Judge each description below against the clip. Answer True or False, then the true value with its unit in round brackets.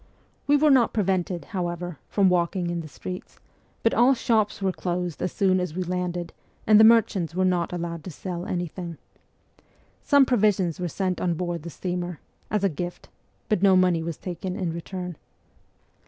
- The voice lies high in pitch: False (180 Hz)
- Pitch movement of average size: False (2.2 semitones)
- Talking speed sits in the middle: True (180 wpm)